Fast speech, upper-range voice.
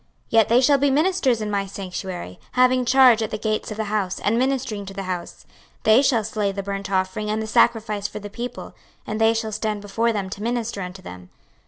Yes: fast, 225 wpm; high, 215 Hz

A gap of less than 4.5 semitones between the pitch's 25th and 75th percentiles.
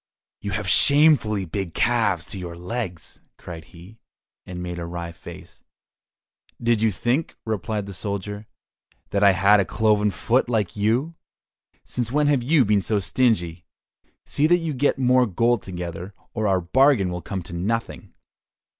No: average, 5.1 semitones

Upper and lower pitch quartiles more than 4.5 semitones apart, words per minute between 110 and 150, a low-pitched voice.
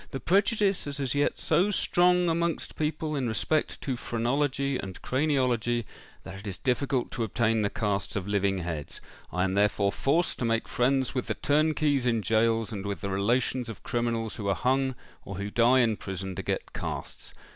No: wide, 5.5 semitones; average, 190 wpm; low, 120 Hz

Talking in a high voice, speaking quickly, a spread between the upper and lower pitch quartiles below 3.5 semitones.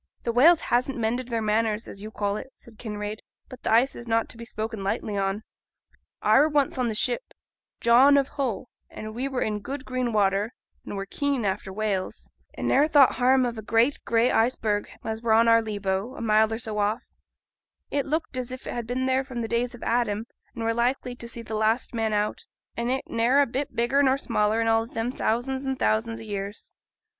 Yes: high, 230 Hz; fast, 225 wpm; average, 2.9 semitones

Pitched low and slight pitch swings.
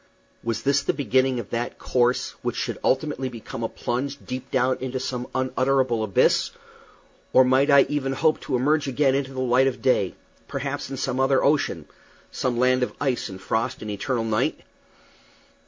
Yes: low, 130 Hz; narrow, 1.7 semitones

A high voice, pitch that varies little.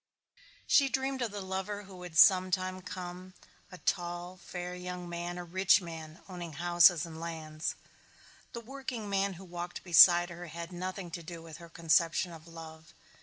No: medium, 175 Hz; narrow, 1.8 semitones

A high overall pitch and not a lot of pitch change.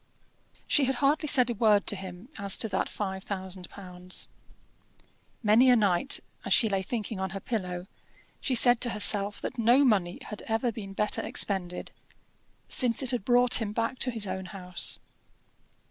No: high, 210 Hz; average, 4.1 semitones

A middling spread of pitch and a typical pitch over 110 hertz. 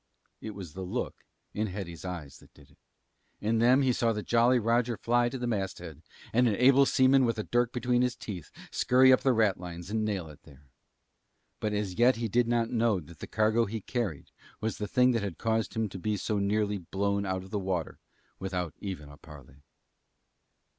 No: average, 4.4 semitones; low, 105 Hz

